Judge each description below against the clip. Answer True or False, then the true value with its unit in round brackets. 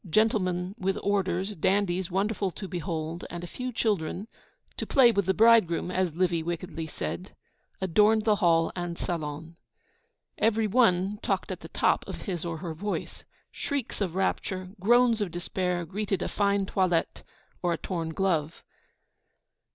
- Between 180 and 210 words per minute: False (150 wpm)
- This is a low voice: False (185 Hz)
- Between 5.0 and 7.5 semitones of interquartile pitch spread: False (3.2 semitones)